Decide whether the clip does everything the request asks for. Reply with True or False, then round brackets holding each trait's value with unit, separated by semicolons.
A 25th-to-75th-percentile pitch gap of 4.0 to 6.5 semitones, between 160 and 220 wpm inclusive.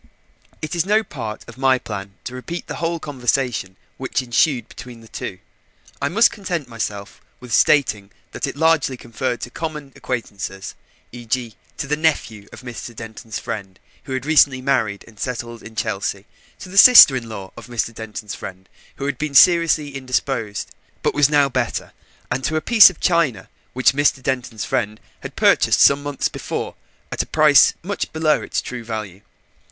True (5.1 semitones; 175 wpm)